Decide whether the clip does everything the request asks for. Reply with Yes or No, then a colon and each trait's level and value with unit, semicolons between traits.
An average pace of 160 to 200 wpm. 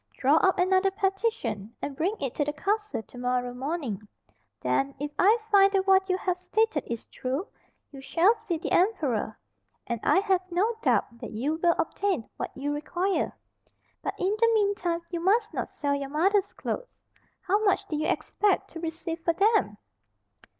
Yes: average, 180 wpm